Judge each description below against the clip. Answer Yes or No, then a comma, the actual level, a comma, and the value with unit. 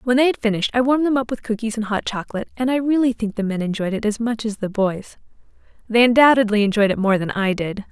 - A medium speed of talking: No, fast, 260 wpm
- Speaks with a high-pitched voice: Yes, high, 225 Hz